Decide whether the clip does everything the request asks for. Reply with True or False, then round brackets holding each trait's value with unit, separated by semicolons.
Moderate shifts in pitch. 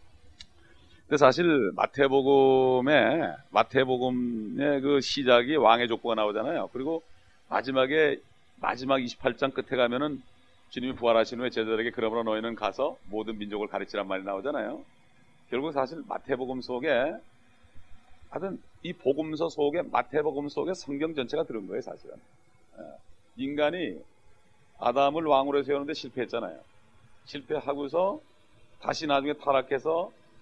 True (4.1 semitones)